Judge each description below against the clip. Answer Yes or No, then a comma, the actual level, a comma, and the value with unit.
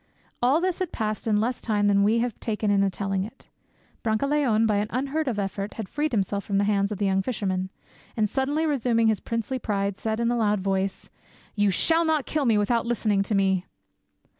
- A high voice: Yes, high, 215 Hz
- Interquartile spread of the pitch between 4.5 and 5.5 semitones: No, average, 3.7 semitones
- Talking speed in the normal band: No, fast, 210 wpm